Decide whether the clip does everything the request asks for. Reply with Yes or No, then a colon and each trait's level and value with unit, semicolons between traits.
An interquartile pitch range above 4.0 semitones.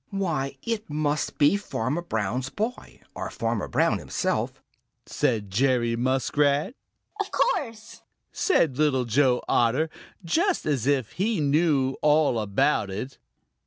Yes: average, 5.2 semitones